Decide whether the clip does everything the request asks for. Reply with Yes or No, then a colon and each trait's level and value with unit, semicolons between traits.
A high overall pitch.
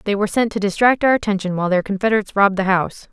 Yes: high, 205 Hz